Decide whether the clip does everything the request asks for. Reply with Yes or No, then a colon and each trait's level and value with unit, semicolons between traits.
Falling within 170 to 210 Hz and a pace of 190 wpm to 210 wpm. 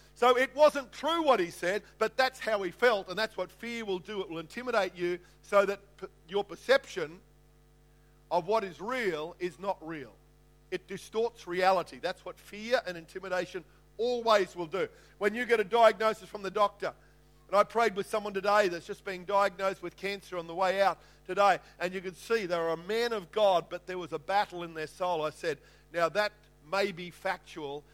Yes: high, 190 Hz; average, 200 wpm